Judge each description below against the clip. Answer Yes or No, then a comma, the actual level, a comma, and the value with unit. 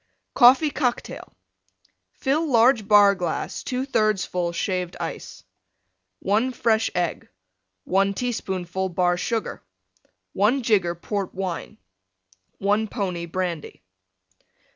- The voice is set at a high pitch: Yes, high, 200 Hz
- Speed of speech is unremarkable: No, slow, 100 wpm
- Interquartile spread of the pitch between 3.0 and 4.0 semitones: No, average, 4.4 semitones